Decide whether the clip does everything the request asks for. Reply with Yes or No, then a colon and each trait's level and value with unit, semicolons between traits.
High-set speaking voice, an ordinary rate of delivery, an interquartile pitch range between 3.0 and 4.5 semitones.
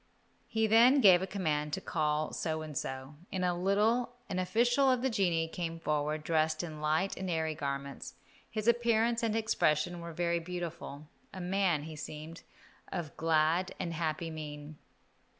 No: medium, 170 Hz; average, 165 wpm; average, 4.1 semitones